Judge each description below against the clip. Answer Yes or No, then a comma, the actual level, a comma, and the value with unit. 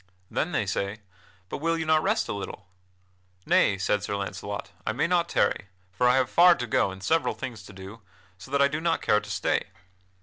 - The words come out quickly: Yes, fast, 215 wpm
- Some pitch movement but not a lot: No, wide, 7.9 semitones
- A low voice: Yes, low, 120 Hz